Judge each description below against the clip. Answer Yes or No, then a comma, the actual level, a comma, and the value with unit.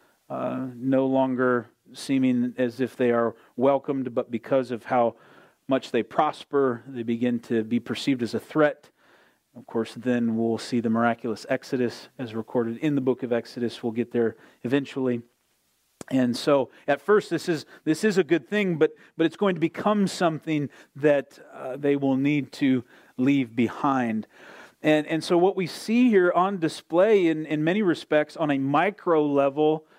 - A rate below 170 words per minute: No, average, 180 wpm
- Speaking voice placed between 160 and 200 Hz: No, low, 135 Hz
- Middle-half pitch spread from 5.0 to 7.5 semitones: No, average, 4.3 semitones